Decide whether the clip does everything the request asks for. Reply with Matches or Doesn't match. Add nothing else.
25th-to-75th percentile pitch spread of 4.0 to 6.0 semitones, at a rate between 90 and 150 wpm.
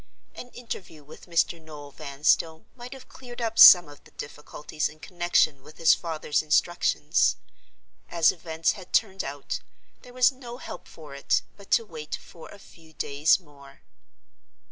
Doesn't match